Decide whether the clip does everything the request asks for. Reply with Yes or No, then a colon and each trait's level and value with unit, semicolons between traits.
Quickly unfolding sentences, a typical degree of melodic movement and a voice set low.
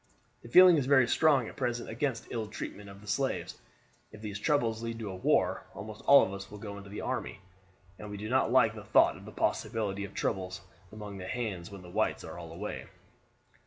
Yes: fast, 215 wpm; average, 3.2 semitones; low, 105 Hz